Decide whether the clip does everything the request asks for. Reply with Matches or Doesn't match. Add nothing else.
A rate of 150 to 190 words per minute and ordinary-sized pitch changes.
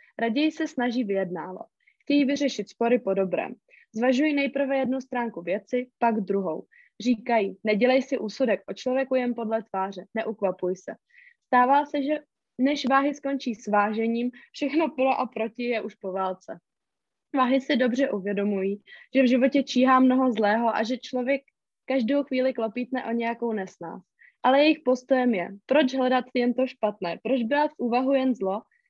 Matches